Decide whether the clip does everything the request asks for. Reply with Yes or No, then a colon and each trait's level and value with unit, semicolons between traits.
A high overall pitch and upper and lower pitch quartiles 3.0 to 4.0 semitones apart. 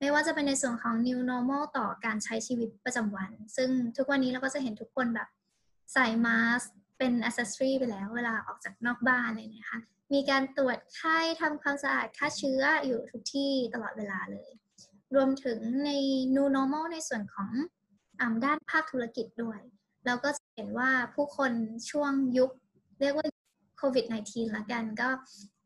Yes: very high, 250 Hz; average, 3.3 semitones